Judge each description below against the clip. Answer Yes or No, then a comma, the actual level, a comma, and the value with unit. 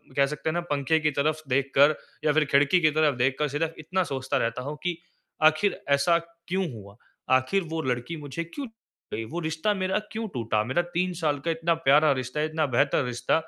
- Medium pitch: Yes, medium, 155 Hz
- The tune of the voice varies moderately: Yes, average, 3.7 semitones